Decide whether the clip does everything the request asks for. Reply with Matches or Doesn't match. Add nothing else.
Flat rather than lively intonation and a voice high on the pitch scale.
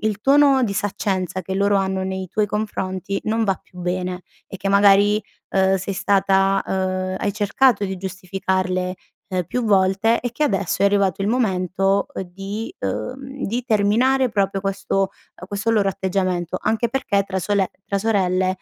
Matches